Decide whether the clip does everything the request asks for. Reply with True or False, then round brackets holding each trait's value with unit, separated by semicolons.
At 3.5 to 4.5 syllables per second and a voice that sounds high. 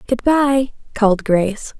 True (4.3 syllables/s; 235 Hz)